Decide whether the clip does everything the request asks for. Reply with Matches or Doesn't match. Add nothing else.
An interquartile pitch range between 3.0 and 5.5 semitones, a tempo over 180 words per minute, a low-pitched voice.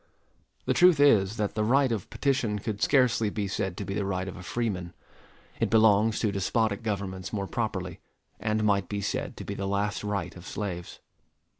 Doesn't match